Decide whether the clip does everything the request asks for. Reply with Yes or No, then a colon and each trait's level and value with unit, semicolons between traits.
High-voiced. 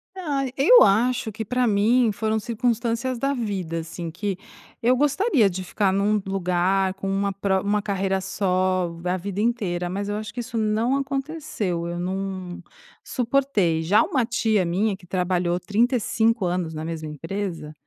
Yes: high, 200 Hz